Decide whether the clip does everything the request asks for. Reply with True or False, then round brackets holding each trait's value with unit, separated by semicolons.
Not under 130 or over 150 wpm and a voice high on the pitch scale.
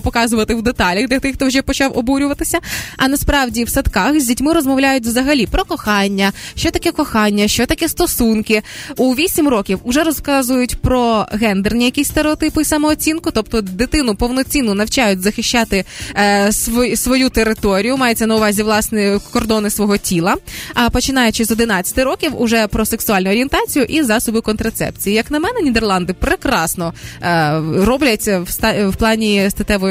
True (145 wpm; 235 Hz)